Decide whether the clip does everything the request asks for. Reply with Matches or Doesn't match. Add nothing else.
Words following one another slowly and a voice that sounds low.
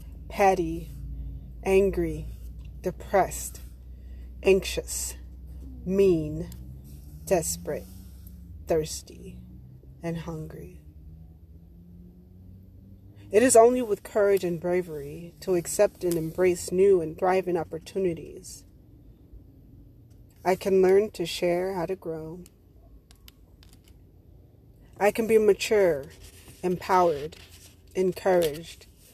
Matches